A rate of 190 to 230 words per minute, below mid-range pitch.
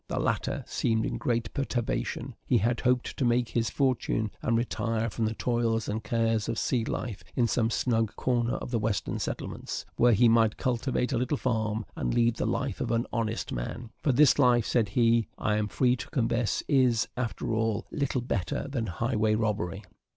Yes: average, 195 wpm; low, 115 Hz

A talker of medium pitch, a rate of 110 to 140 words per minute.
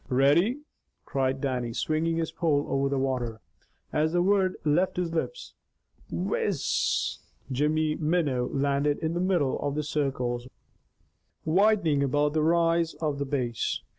Yes: medium, 150 Hz; slow, 135 wpm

